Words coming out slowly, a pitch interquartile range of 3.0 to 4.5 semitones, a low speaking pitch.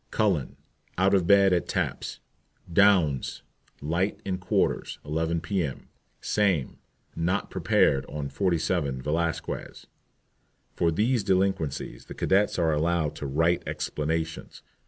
Yes: slow, 115 wpm; average, 4.0 semitones; very low, 85 Hz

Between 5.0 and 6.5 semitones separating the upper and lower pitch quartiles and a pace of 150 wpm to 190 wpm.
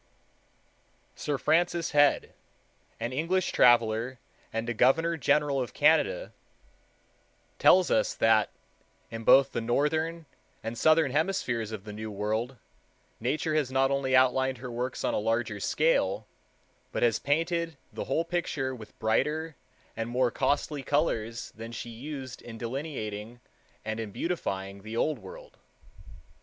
No: average, 5.3 semitones; slow, 135 wpm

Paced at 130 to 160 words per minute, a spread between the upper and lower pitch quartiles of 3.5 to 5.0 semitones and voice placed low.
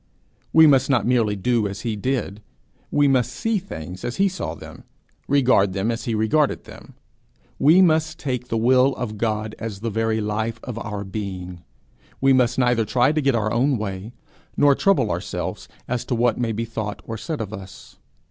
No: average, 190 wpm; average, 3.8 semitones; low, 115 Hz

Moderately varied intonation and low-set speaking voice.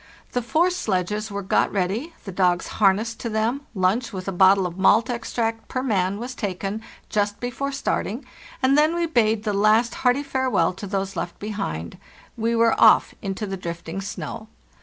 No: average, 4.1 semitones; high, 215 Hz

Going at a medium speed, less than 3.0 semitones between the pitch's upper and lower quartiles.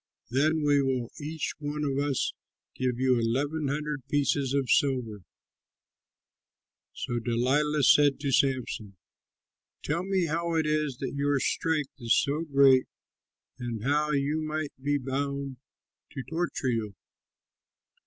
No: slow, 130 wpm; narrow, 2.6 semitones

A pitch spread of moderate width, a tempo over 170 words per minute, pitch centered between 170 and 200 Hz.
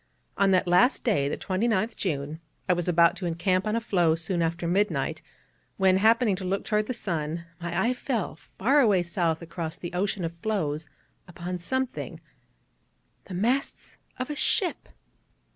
No: average, 4.2 semitones; average, 165 wpm; medium, 185 Hz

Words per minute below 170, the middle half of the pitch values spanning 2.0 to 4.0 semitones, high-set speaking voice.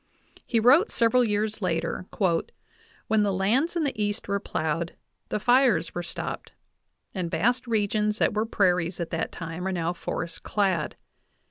No: average, 160 wpm; average, 4.4 semitones; high, 205 Hz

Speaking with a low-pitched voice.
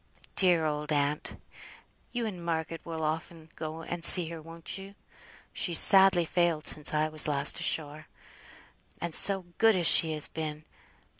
No: medium, 160 Hz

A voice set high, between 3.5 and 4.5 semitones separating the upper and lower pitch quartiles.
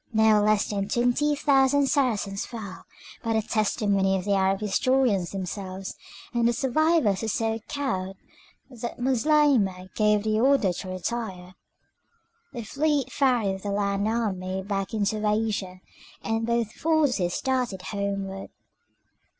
Yes: high, 215 Hz; average, 4.1 semitones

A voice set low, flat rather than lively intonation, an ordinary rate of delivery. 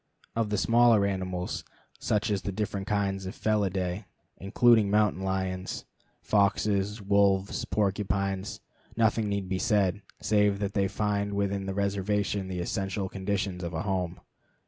Yes: low, 100 Hz; narrow, 1.5 semitones; average, 145 wpm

